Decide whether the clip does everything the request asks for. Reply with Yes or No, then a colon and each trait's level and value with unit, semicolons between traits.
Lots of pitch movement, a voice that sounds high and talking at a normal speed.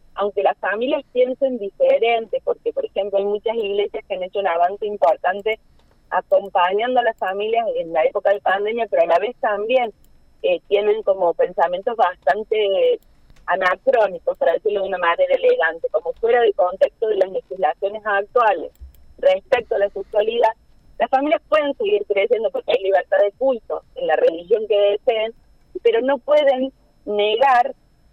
Yes: wide, 7.0 semitones; high, 230 Hz; average, 160 wpm